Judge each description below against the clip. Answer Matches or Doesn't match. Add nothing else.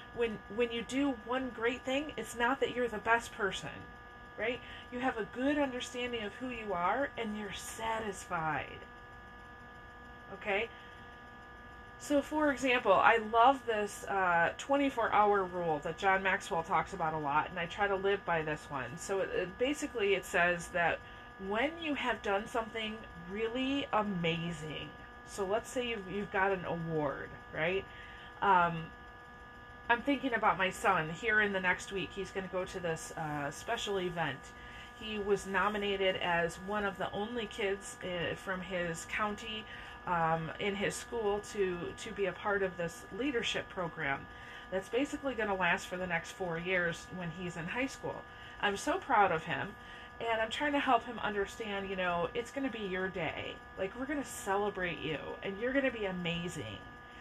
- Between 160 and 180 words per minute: Matches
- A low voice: Doesn't match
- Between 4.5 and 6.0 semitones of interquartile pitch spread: Matches